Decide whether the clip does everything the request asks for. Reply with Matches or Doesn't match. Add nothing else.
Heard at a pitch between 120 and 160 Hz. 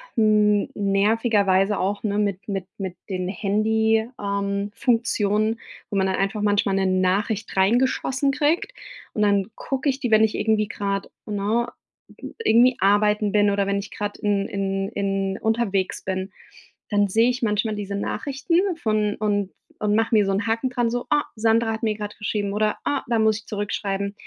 Doesn't match